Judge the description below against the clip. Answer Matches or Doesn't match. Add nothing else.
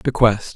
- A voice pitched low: Matches